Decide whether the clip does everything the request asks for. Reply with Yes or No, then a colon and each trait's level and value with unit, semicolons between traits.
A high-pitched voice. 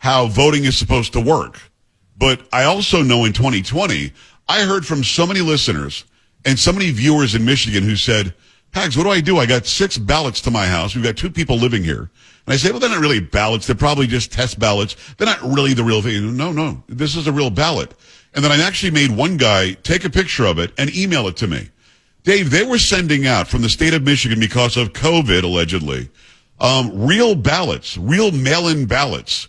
No: low, 130 Hz